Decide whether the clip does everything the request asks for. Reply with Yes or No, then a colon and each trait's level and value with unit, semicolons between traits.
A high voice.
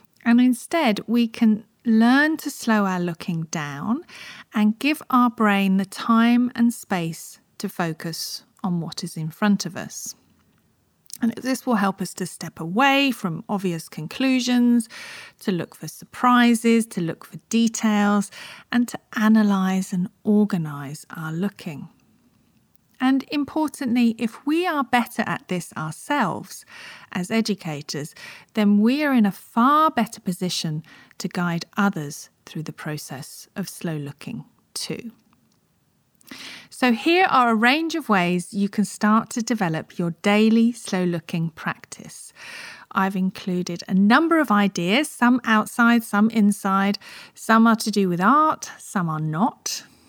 Yes: high, 210 Hz